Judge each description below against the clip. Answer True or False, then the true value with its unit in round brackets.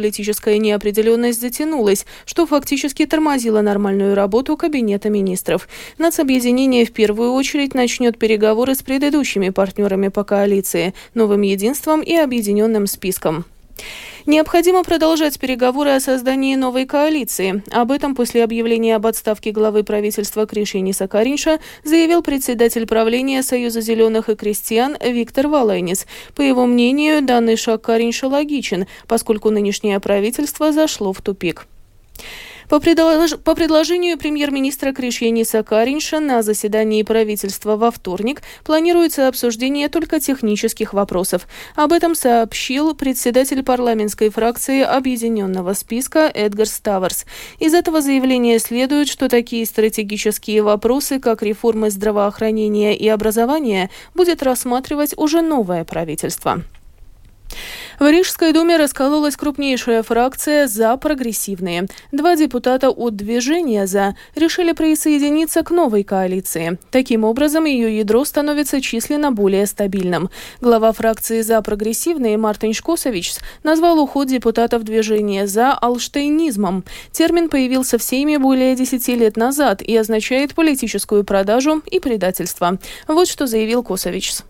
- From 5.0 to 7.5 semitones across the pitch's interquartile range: True (5.3 semitones)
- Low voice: False (235 Hz)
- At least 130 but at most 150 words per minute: False (115 wpm)